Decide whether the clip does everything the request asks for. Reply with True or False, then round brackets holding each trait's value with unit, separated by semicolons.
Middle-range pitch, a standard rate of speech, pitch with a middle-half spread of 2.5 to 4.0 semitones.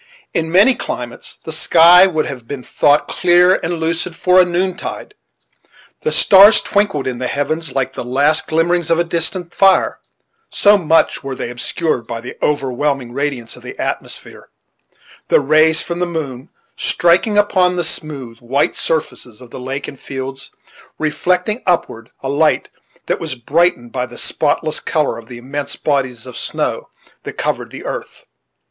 False (155 Hz; 160 wpm; 5.0 semitones)